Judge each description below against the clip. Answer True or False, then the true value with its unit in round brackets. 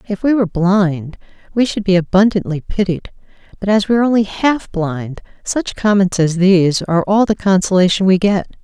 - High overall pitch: True (195 Hz)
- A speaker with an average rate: True (180 wpm)